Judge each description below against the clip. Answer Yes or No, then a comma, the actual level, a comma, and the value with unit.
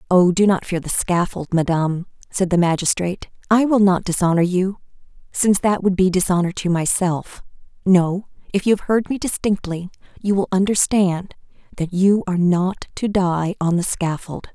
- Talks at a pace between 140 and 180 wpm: Yes, average, 170 wpm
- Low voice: No, medium, 185 Hz